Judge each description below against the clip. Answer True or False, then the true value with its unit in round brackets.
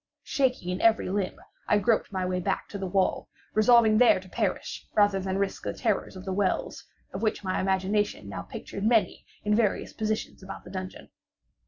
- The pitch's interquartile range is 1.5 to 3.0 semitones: True (2.4 semitones)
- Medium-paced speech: True (185 wpm)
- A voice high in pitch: True (200 Hz)